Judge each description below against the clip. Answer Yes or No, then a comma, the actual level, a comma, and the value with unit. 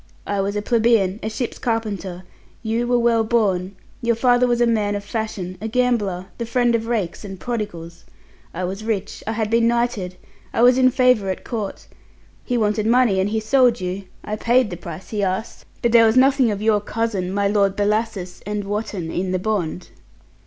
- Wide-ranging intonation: No, average, 3.3 semitones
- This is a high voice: Yes, high, 215 Hz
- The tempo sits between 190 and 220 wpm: Yes, average, 195 wpm